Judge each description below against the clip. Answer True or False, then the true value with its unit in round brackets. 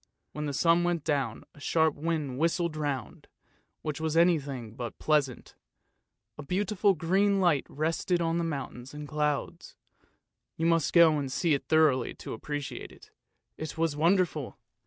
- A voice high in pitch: False (155 Hz)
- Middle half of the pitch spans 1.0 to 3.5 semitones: True (2.8 semitones)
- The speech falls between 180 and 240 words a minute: False (155 wpm)